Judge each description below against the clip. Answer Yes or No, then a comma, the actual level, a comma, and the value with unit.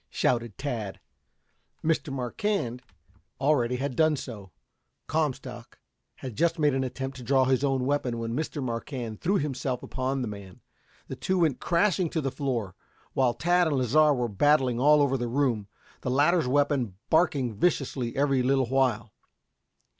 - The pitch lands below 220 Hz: Yes, low, 135 Hz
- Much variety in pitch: No, average, 3.3 semitones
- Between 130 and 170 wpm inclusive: Yes, average, 155 wpm